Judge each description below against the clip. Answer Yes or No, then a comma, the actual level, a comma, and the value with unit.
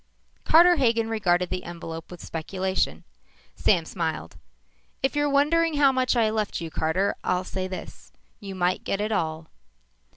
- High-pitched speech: Yes, high, 195 Hz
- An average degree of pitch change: No, wide, 6.6 semitones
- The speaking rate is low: No, average, 155 wpm